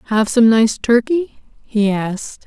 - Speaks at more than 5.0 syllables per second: No, 3.9 syllables/s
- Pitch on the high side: Yes, high, 230 Hz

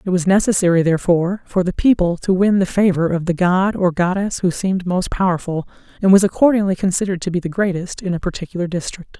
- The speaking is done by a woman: Yes, female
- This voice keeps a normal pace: No, fast, 210 wpm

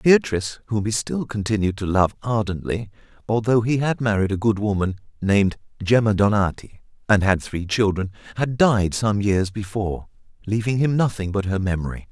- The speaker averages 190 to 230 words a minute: No, average, 165 wpm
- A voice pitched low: Yes, low, 105 Hz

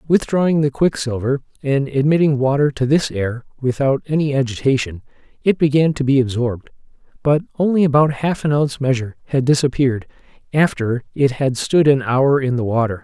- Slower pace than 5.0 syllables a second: No, 5.6 syllables/s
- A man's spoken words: Yes, male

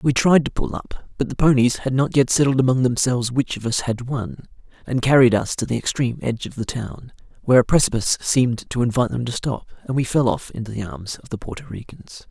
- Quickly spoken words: Yes, fast, 240 wpm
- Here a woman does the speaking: No, male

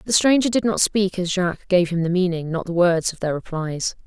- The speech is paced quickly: Yes, fast, 250 wpm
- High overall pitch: No, medium, 180 Hz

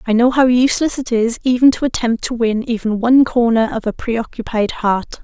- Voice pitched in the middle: No, high, 235 Hz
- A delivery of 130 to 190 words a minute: No, fast, 205 wpm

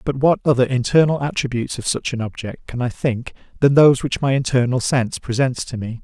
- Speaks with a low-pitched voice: Yes, low, 130 Hz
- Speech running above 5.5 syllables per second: Yes, 5.9 syllables/s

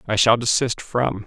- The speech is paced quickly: No, average, 190 wpm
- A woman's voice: No, male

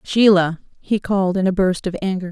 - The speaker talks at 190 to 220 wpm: Yes, fast, 205 wpm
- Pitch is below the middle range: No, high, 190 Hz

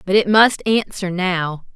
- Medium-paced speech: Yes, average, 170 wpm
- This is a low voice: No, high, 195 Hz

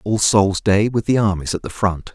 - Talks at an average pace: No, fast, 250 wpm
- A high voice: No, low, 100 Hz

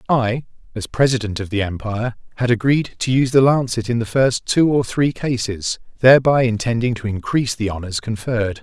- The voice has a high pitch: No, low, 120 Hz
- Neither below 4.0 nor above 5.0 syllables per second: No, 5.6 syllables/s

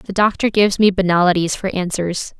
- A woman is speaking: Yes, female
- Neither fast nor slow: Yes, average, 175 wpm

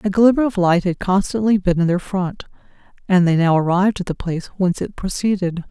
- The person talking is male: No, female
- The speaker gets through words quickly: Yes, fast, 210 wpm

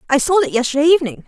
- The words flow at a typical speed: No, fast, 235 wpm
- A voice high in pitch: Yes, very high, 275 Hz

